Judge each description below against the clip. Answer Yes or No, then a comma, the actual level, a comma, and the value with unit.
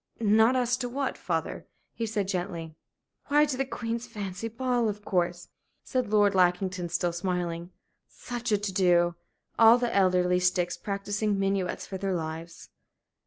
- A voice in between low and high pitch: No, high, 200 Hz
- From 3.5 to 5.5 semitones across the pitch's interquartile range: Yes, average, 4.3 semitones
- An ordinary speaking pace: Yes, average, 155 wpm